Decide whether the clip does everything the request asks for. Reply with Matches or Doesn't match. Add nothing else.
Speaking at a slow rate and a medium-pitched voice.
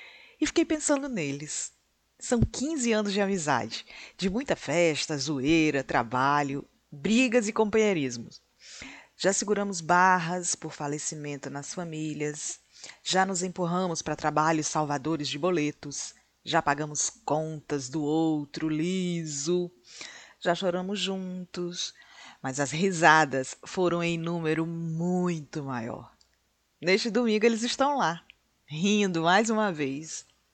Matches